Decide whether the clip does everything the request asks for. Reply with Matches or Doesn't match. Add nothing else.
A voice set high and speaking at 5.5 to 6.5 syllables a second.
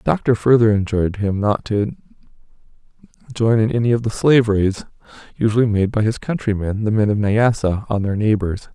Doesn't match